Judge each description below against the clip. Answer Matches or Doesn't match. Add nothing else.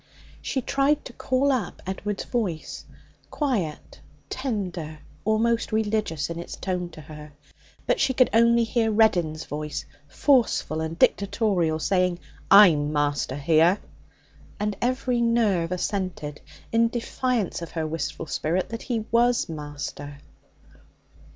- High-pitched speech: Matches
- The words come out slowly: Matches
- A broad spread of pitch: Matches